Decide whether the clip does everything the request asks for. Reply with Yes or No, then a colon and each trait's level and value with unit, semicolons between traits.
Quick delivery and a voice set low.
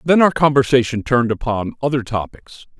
No: average, 150 wpm; low, 130 Hz